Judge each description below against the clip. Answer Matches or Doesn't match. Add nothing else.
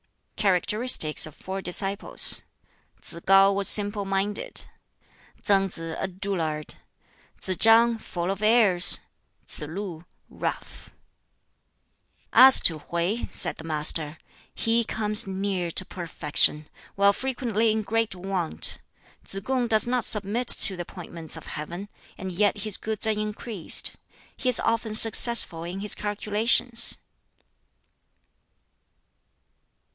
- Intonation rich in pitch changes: Doesn't match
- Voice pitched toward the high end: Matches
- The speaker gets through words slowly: Matches